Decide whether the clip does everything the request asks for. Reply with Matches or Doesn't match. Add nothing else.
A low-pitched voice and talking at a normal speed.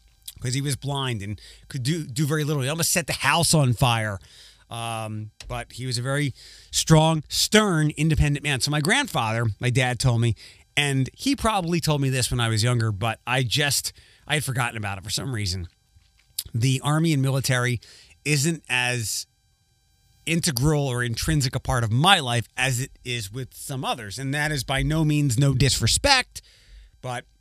Matches